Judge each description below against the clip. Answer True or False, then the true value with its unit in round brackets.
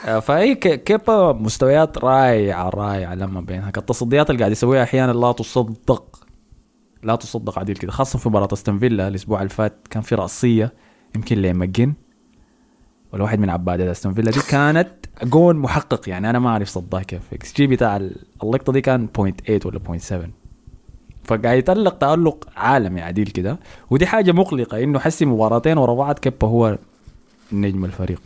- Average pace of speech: False (160 wpm)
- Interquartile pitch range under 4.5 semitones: False (5.0 semitones)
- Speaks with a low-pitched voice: True (115 Hz)